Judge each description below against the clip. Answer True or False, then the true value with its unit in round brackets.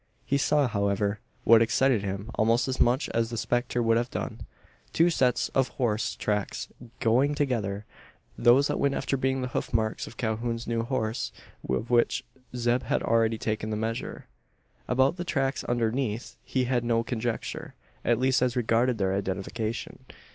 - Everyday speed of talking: True (165 wpm)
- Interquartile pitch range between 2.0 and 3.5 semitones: True (2.6 semitones)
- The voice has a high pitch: False (120 Hz)